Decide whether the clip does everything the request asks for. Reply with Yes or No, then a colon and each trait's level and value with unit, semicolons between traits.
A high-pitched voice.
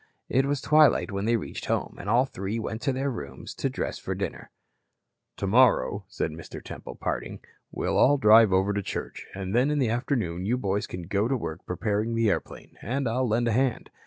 No: low, 115 Hz